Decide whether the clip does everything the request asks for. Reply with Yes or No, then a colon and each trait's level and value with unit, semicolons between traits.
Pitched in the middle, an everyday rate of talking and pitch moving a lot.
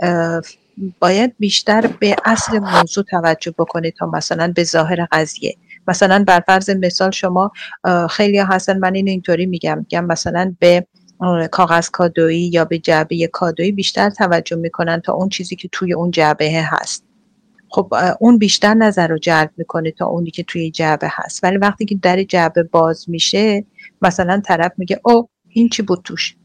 No: medium, 180 Hz; average, 165 wpm; average, 2.9 semitones